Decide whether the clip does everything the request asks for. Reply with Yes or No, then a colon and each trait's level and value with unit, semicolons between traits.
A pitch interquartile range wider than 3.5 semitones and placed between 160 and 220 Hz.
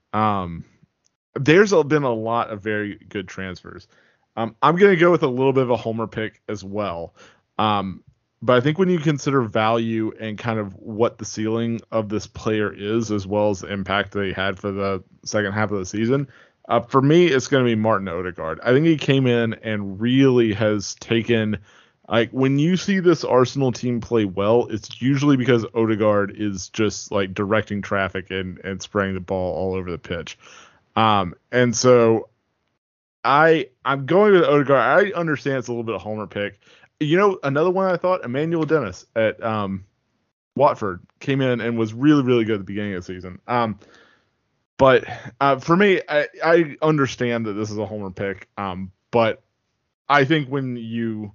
No: average, 4.7 semitones; low, 115 Hz